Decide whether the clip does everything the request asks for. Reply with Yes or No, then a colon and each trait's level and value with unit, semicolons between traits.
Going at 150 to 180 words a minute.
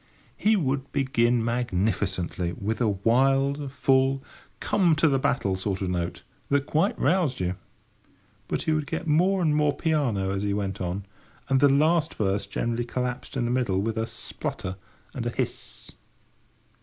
Yes: average, 170 wpm